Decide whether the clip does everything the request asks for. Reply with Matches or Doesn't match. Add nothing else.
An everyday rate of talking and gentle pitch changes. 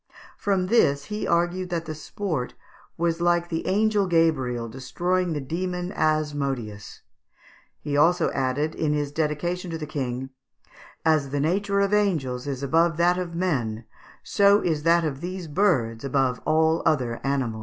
Doesn't match